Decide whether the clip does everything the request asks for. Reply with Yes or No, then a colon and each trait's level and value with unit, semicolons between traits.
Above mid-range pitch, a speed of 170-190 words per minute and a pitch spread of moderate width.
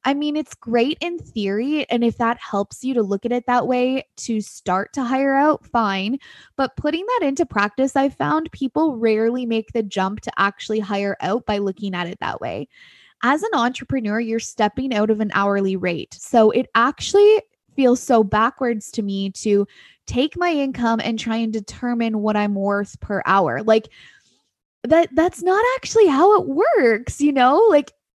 Yes: high, 235 Hz; average, 185 wpm; average, 4.7 semitones